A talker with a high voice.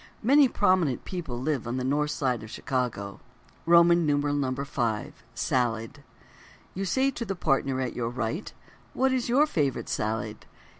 No: medium, 140 Hz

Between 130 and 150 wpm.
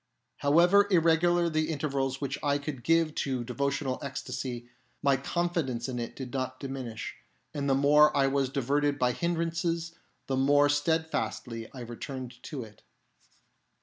Yes: average, 145 wpm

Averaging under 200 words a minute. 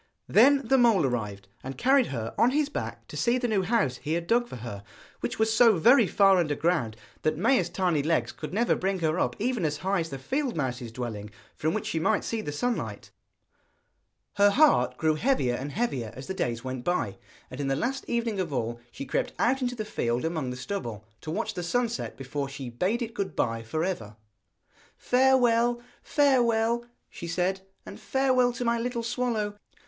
No: fast, 205 wpm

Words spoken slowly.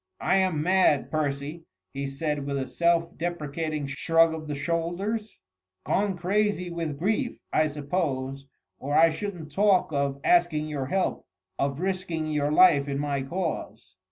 No: average, 150 wpm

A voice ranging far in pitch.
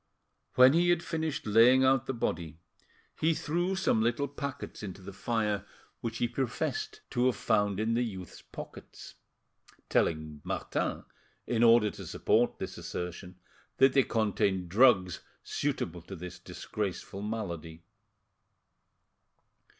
Yes: wide, 5.9 semitones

